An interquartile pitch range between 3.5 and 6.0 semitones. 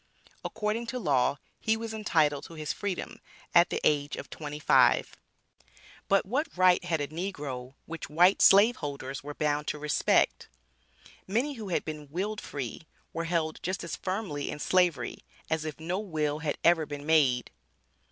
Yes: average, 4.5 semitones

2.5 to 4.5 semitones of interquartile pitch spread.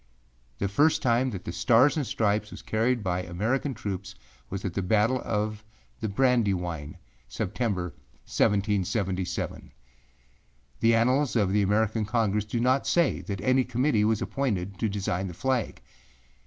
Yes: average, 4.0 semitones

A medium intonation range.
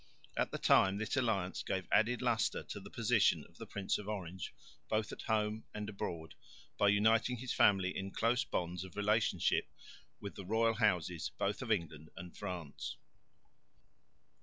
Yes: average, 3.3 semitones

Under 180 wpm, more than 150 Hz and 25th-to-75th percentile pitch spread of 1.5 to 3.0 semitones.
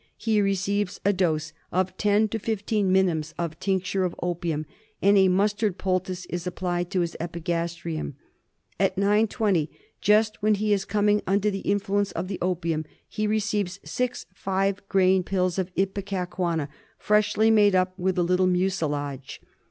Yes: average, 150 wpm; high, 190 Hz; narrow, 2.5 semitones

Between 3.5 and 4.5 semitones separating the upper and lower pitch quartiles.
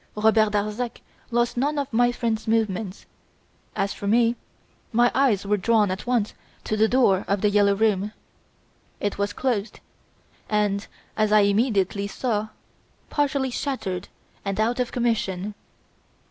No: average, 3.0 semitones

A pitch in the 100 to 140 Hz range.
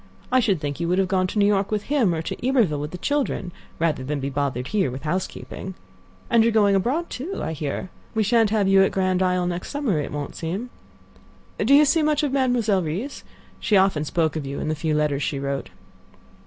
No: high, 190 Hz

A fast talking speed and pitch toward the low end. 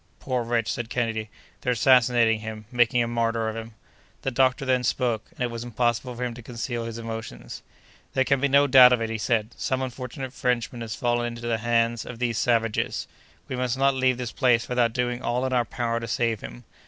Yes: fast, 215 wpm; low, 120 Hz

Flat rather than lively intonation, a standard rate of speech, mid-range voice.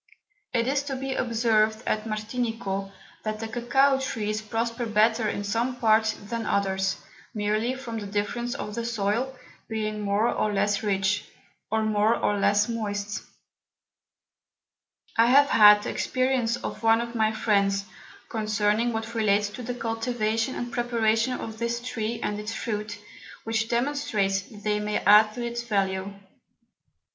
No: narrow, 2.2 semitones; average, 150 wpm; high, 220 Hz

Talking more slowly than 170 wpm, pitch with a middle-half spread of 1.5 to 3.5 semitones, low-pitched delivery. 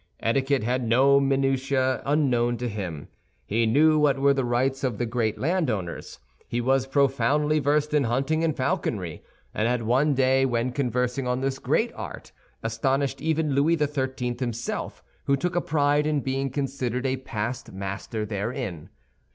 Yes: average, 160 wpm; average, 2.8 semitones; low, 130 Hz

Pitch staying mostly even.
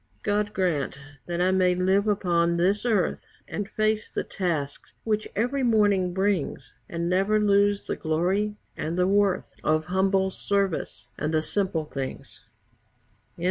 No: average, 3.1 semitones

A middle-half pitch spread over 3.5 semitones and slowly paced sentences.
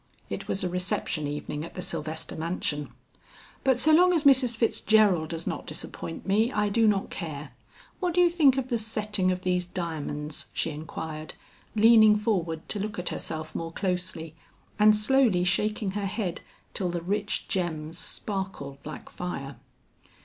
No: average, 4.9 semitones; average, 165 wpm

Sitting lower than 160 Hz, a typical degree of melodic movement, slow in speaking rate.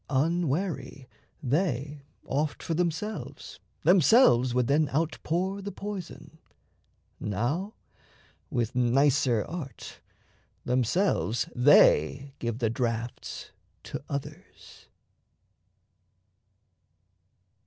No: medium, 140 Hz; wide, 5.7 semitones; slow, 75 wpm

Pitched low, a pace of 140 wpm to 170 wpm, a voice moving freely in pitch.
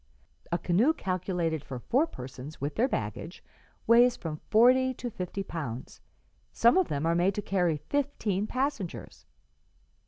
No: medium, 185 Hz; average, 145 wpm; wide, 7.4 semitones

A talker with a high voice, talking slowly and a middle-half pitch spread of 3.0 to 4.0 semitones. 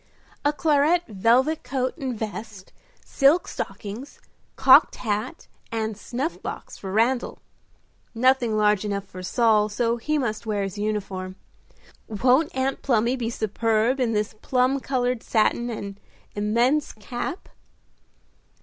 Yes: high, 230 Hz; slow, 125 wpm; average, 3.7 semitones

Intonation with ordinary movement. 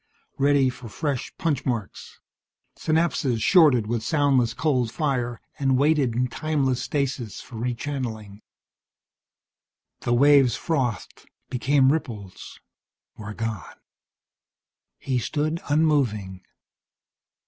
Yes: average, 3.9 semitones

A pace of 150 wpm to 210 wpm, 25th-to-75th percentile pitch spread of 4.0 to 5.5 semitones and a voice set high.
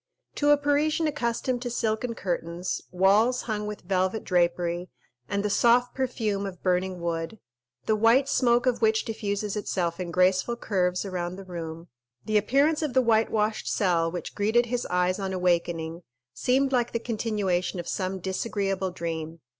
Yes: average, 160 wpm; average, 4.7 semitones; high, 200 Hz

